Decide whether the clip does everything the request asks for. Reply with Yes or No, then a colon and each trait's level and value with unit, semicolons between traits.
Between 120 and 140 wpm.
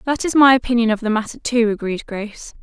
No: fast, 230 wpm